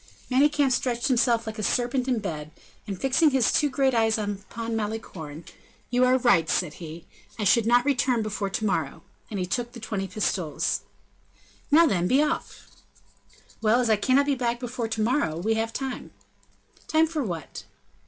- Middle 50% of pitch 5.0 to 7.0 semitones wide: No, average, 4.4 semitones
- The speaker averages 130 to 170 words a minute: No, average, 180 wpm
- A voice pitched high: Yes, high, 230 Hz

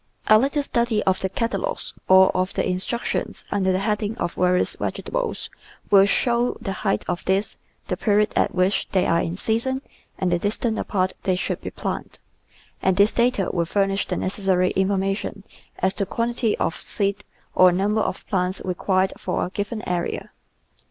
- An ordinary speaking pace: Yes, average, 175 wpm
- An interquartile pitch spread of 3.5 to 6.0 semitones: No, average, 3.0 semitones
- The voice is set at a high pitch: Yes, high, 195 Hz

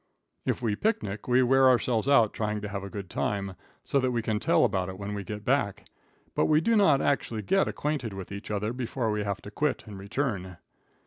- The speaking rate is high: Yes, fast, 220 wpm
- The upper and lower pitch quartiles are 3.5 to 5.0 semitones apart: Yes, average, 4.4 semitones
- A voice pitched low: Yes, low, 110 Hz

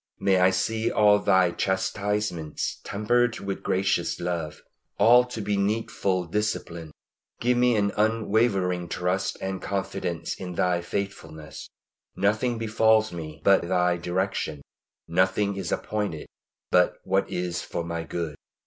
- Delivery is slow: Yes, slow, 130 wpm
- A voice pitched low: Yes, very low, 95 Hz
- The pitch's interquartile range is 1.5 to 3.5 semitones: Yes, average, 3.2 semitones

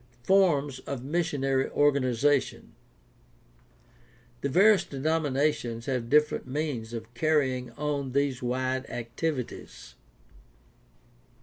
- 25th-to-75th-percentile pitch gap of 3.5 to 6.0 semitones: No, average, 2.9 semitones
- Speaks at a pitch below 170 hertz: Yes, medium, 140 Hz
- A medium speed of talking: No, slow, 90 wpm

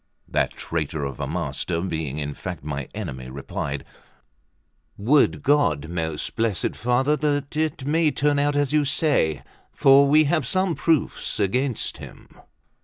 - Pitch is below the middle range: Yes, low, 125 Hz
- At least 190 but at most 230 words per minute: No, average, 145 wpm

